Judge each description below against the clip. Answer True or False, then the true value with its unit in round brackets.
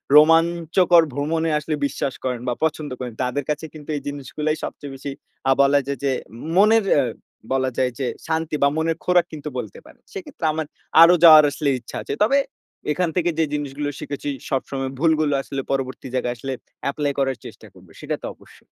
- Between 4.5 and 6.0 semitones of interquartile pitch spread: False (3.1 semitones)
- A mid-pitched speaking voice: True (150 Hz)